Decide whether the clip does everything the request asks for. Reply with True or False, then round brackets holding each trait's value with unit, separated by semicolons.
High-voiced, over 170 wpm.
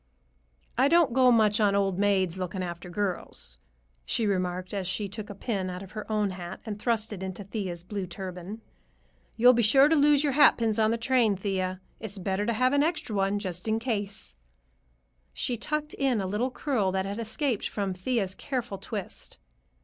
True (205 Hz; 190 wpm)